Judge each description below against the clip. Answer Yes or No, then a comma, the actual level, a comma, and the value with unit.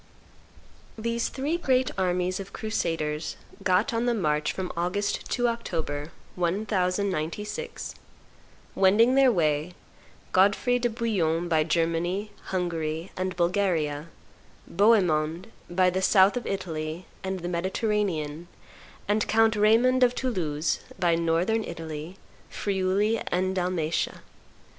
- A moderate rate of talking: No, slow, 110 wpm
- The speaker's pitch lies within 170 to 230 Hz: Yes, medium, 185 Hz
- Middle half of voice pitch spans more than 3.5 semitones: Yes, average, 4.5 semitones